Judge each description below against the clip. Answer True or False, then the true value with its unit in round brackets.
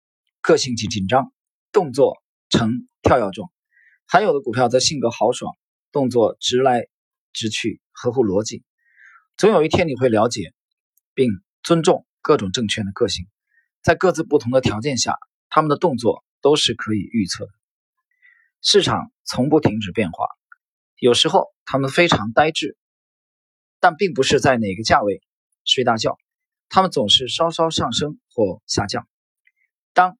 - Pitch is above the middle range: False (165 Hz)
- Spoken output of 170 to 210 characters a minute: False (225 characters per minute)